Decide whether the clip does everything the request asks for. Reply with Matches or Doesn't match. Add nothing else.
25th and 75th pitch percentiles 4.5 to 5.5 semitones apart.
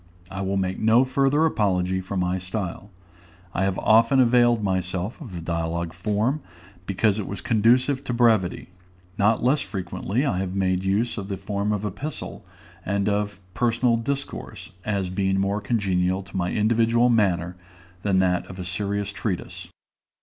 Doesn't match